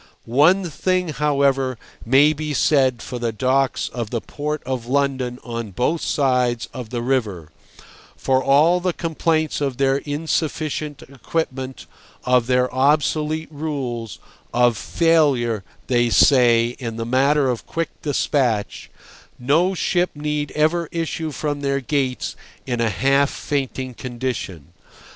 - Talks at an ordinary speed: No, slow, 130 wpm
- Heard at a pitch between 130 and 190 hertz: Yes, low, 135 Hz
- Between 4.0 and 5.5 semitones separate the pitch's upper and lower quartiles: No, average, 3.6 semitones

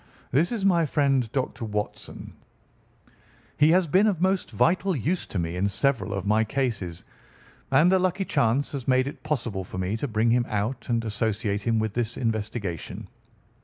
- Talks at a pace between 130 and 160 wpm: No, average, 175 wpm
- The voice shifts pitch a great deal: Yes, wide, 6.1 semitones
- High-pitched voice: No, low, 120 Hz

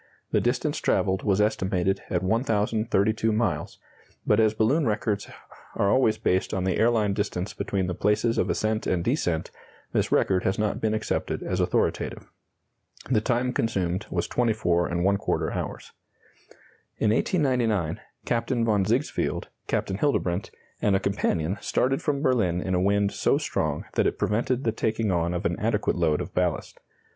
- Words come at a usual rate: Yes, average, 155 wpm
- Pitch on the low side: Yes, low, 105 Hz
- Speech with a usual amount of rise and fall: Yes, average, 3.4 semitones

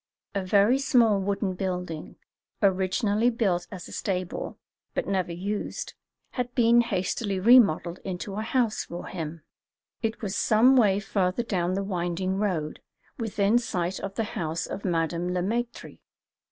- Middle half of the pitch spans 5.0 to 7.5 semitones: No, average, 3.7 semitones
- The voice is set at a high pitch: Yes, high, 195 Hz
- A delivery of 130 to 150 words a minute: Yes, average, 145 wpm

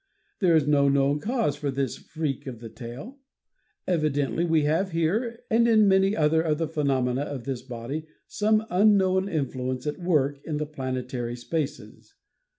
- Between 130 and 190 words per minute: Yes, average, 160 wpm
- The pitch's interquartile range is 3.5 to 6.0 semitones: Yes, average, 5.2 semitones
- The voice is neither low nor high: Yes, medium, 150 Hz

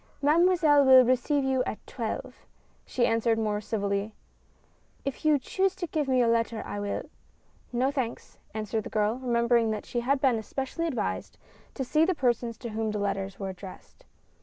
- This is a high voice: Yes, high, 240 Hz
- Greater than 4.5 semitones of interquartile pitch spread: No, average, 4.0 semitones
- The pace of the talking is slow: No, average, 185 wpm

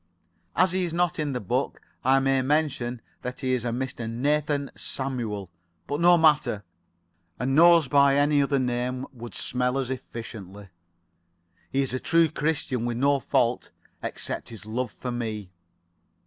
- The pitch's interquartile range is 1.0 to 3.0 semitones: No, average, 3.4 semitones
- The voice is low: Yes, low, 130 Hz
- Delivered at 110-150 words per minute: No, average, 160 wpm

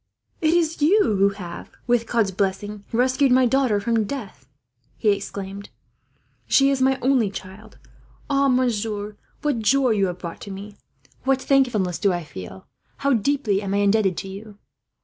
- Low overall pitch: No, high, 215 Hz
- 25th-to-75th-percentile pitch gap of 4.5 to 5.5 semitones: Yes, average, 4.9 semitones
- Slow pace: No, average, 165 wpm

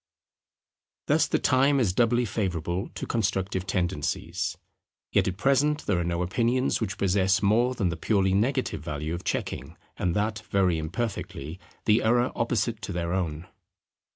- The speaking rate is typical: Yes, average, 155 wpm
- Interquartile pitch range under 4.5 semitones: No, average, 5.1 semitones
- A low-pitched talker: Yes, low, 100 Hz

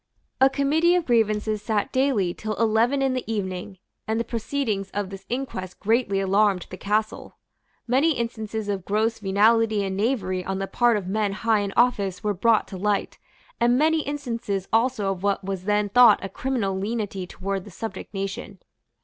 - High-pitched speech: Yes, high, 215 Hz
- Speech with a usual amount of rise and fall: Yes, average, 3.4 semitones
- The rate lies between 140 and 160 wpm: No, average, 175 wpm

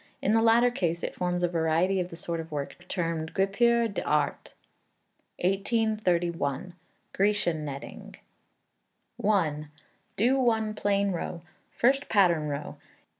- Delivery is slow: Yes, slow, 125 wpm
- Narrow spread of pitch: No, average, 4.5 semitones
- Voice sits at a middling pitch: Yes, medium, 180 Hz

